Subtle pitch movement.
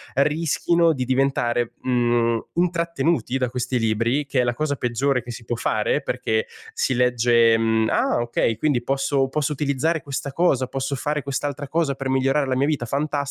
No: average, 3.2 semitones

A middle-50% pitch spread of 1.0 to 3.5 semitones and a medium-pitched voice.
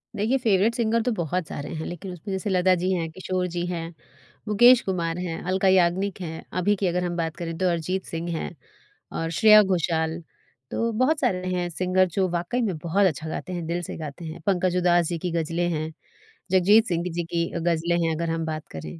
Yes: narrow, 2.4 semitones; medium, 175 Hz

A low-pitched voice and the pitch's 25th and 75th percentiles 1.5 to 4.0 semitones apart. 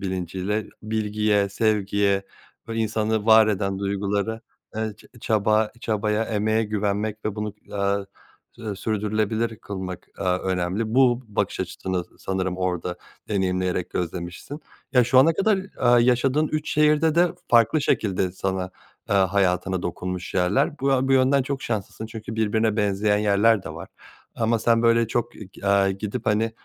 Yes: low, 105 Hz; average, 2.8 semitones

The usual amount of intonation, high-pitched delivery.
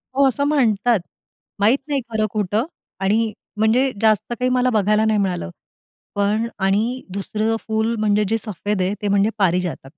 No: narrow, 2.3 semitones; high, 215 Hz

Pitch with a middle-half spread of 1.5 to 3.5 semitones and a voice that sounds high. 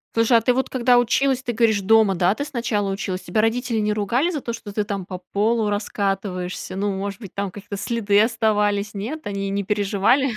Yes: average, 2.8 semitones; high, 210 Hz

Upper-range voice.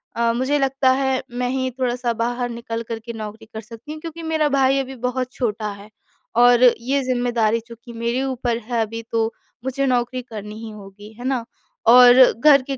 Yes: high, 245 Hz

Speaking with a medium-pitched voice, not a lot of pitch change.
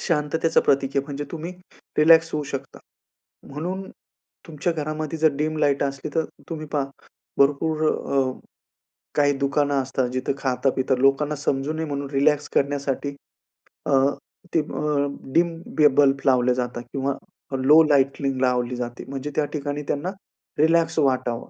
Yes: medium, 145 Hz; narrow, 2.2 semitones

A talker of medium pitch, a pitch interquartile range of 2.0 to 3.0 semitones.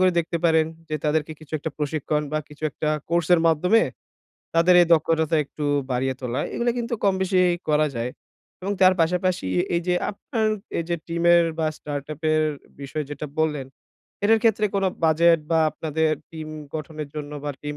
Yes: medium, 160 Hz; narrow, 2.6 semitones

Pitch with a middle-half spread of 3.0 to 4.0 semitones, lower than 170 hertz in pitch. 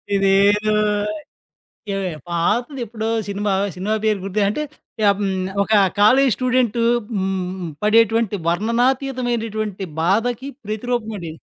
No: average, 3.4 semitones; high, 215 Hz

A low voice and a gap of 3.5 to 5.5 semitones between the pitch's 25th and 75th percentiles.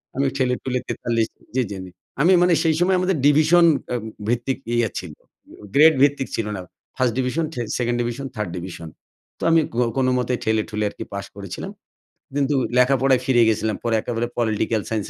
Yes: low, 125 Hz; average, 4.0 semitones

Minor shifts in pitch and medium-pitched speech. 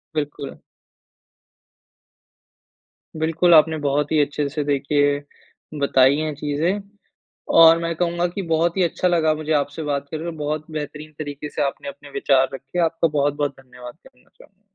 Yes: narrow, 2.2 semitones; medium, 150 Hz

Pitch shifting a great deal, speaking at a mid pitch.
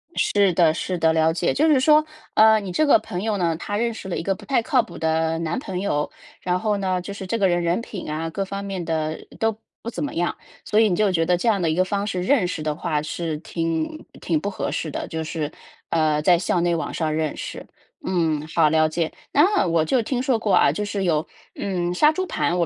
No: average, 4.3 semitones; medium, 180 Hz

